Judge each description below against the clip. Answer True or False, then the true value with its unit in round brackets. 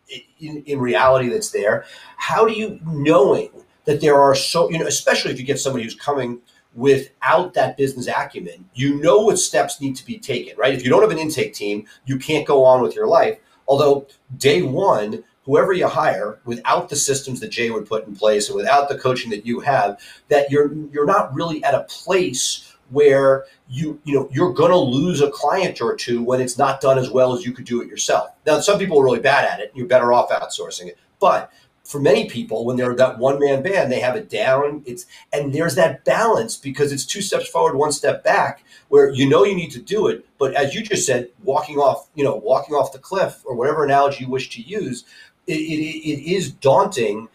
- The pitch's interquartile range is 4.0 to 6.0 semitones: False (3.4 semitones)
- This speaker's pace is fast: True (225 wpm)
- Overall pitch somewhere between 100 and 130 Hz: False (140 Hz)